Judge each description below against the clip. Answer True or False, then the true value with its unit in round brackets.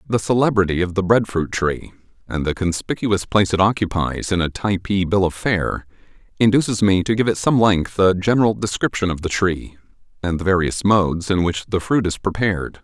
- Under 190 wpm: False (195 wpm)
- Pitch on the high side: False (95 Hz)